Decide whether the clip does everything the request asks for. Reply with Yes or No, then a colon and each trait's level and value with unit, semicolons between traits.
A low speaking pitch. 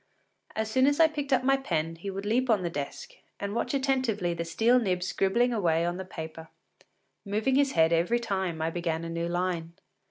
No: high, 190 Hz